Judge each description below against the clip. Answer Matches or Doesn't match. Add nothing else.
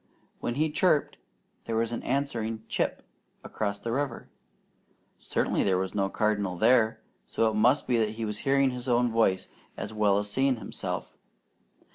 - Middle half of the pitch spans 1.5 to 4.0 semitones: Matches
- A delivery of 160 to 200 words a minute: Matches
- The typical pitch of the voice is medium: Doesn't match